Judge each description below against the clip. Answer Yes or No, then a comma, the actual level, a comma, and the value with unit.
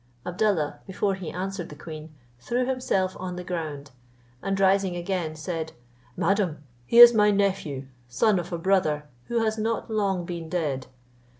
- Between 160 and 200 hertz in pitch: Yes, medium, 185 Hz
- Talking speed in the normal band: Yes, average, 160 wpm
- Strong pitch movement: No, average, 3.9 semitones